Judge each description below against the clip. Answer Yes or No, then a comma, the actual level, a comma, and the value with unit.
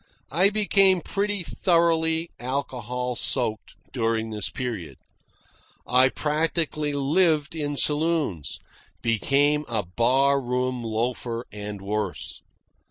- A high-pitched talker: No, low, 135 Hz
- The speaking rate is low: Yes, slow, 100 wpm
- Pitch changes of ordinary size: No, wide, 5.7 semitones